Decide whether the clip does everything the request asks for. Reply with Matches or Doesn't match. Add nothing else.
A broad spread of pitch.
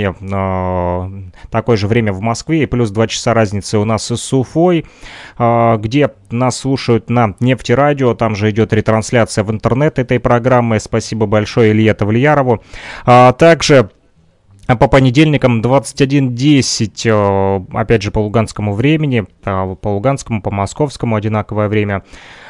Doesn't match